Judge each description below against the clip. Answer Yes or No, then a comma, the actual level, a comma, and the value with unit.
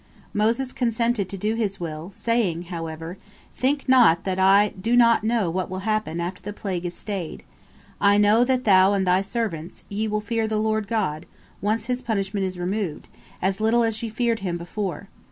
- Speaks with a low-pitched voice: No, high, 205 Hz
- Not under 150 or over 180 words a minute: No, average, 190 wpm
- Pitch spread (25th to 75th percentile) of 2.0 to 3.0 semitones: No, average, 3.5 semitones